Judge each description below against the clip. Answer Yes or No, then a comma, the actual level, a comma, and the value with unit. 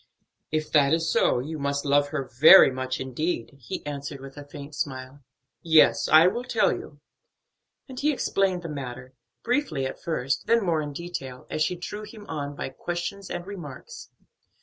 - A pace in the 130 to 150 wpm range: No, average, 175 wpm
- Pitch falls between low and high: Yes, medium, 150 Hz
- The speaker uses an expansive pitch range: No, average, 4.3 semitones